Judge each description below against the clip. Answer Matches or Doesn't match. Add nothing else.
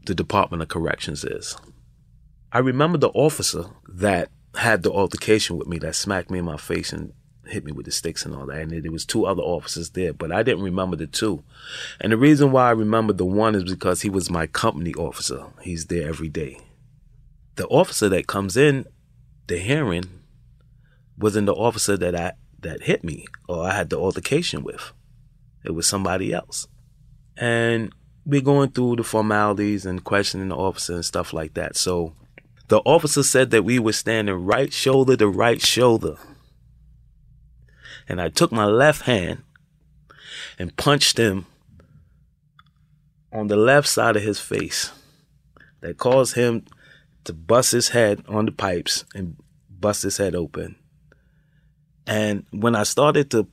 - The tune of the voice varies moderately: Doesn't match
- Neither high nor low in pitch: Doesn't match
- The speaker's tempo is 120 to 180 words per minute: Matches